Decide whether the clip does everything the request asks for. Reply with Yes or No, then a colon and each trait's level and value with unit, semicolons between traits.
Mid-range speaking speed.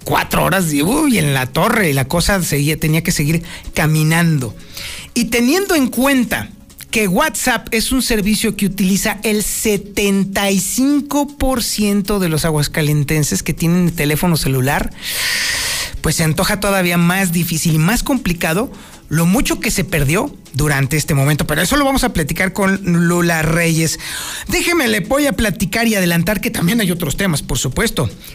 Yes: average, 160 wpm